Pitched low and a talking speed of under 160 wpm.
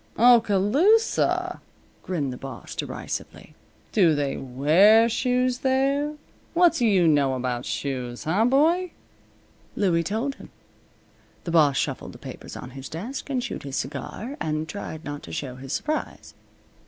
No: medium, 185 Hz; average, 140 wpm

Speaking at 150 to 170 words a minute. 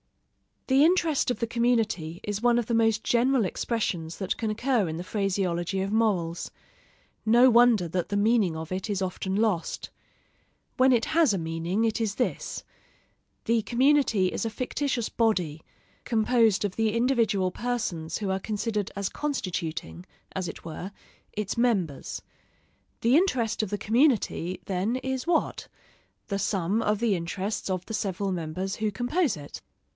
Yes: average, 160 wpm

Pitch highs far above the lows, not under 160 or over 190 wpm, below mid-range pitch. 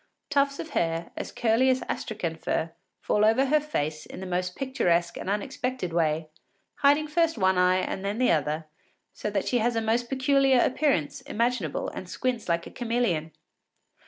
No: wide, 7.0 semitones; average, 170 wpm; high, 220 Hz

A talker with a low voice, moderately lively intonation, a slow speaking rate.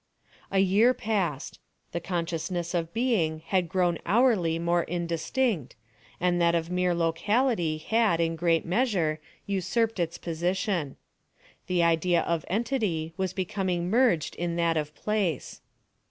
No: medium, 175 Hz; average, 3.3 semitones; slow, 130 wpm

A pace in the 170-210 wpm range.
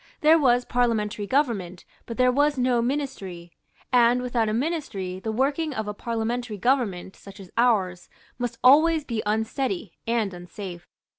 No: average, 150 wpm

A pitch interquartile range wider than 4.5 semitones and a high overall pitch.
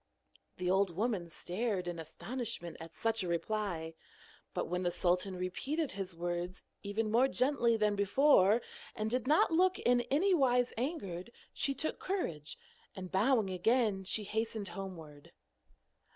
Yes: wide, 5.4 semitones; high, 205 Hz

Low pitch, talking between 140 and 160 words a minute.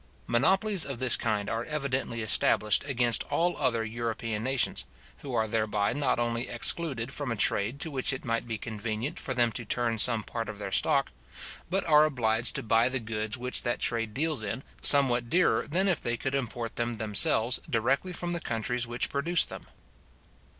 No: low, 120 Hz; average, 185 wpm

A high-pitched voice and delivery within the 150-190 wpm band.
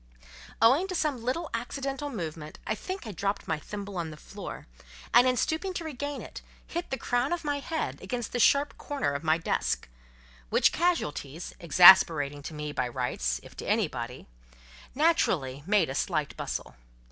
Yes: high, 220 Hz; average, 170 wpm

